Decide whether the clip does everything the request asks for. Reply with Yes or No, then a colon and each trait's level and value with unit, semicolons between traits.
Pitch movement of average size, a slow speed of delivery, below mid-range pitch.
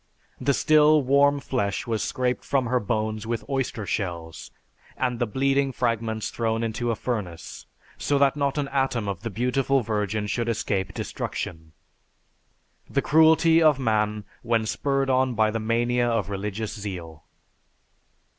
No: average, 4.2 semitones; average, 145 wpm; low, 115 Hz